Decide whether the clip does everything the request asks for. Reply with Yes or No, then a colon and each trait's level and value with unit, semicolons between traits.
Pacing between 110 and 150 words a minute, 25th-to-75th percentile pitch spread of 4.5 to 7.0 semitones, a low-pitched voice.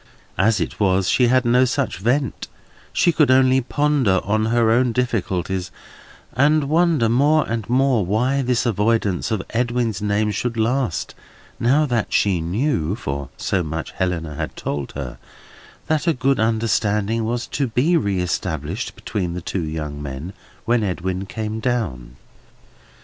Yes: average, 145 wpm; wide, 5.4 semitones; low, 110 Hz